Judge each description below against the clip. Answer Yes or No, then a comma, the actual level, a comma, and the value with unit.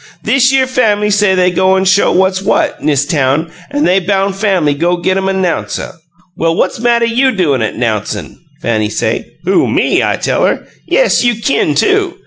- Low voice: No, high, 190 Hz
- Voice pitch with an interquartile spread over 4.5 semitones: Yes, wide, 5.6 semitones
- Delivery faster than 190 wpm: No, average, 180 wpm